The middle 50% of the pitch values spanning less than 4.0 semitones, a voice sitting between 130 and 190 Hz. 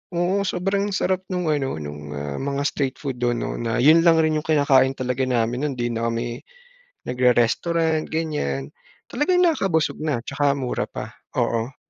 No: average, 5.3 semitones; medium, 140 Hz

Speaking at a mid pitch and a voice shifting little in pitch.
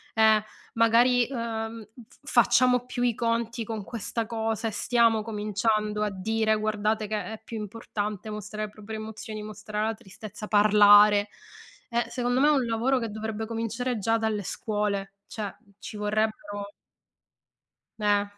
No: high, 220 Hz; narrow, 1.6 semitones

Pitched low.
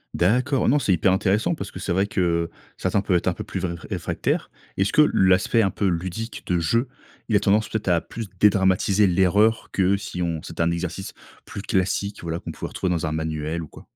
Yes: very low, 95 Hz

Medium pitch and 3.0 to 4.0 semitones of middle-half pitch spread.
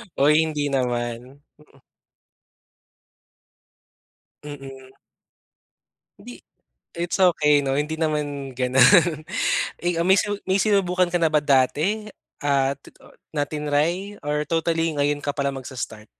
Yes: medium, 150 Hz; average, 3.6 semitones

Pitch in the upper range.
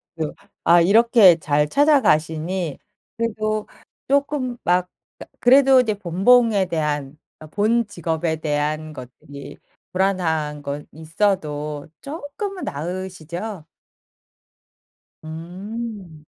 No: medium, 180 Hz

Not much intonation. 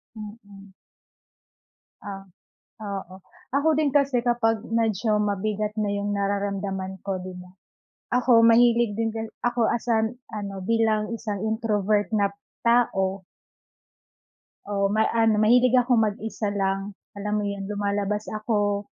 Yes: narrow, 2.2 semitones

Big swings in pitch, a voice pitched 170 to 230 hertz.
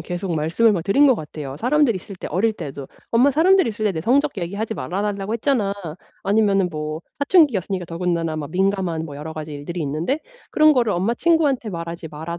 Yes: wide, 6.2 semitones; high, 190 Hz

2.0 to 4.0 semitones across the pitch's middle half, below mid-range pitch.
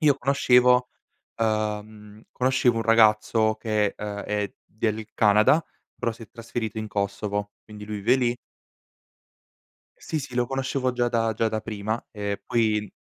Yes: narrow, 2.5 semitones; low, 110 Hz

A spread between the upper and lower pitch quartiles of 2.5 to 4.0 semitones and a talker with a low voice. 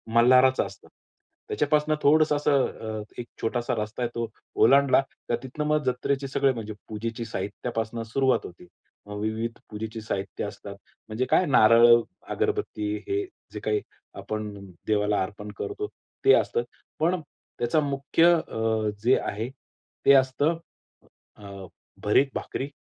No: average, 4.5 semitones; low, 120 Hz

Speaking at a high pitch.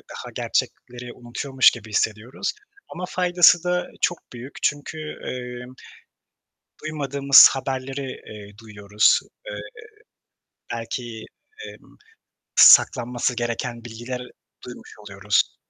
No: low, 125 Hz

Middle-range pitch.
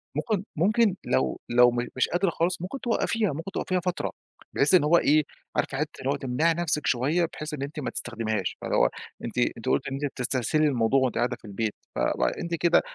Yes: medium, 145 Hz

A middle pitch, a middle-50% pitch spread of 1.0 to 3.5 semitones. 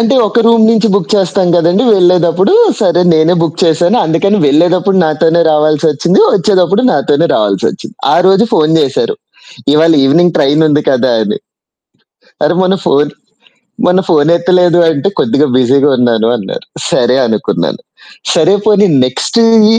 No: medium, 170 Hz; average, 4.2 semitones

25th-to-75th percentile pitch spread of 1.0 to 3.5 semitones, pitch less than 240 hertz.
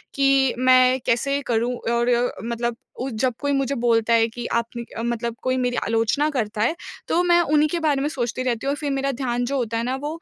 No: average, 2.7 semitones; very high, 250 Hz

